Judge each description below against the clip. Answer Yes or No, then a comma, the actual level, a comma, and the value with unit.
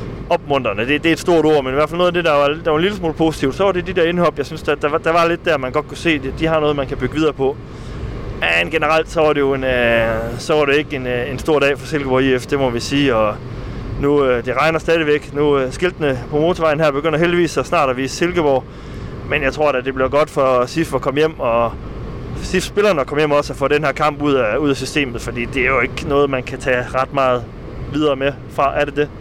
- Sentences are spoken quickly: Yes, fast, 275 wpm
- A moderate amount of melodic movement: Yes, average, 3.1 semitones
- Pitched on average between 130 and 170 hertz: Yes, medium, 140 Hz